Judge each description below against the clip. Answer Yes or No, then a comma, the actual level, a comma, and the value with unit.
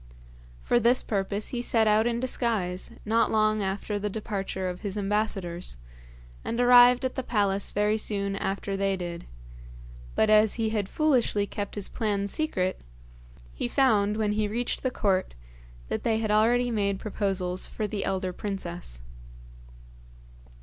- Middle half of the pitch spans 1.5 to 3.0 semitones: Yes, narrow, 2.5 semitones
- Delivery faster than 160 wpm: No, average, 150 wpm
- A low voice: No, high, 210 Hz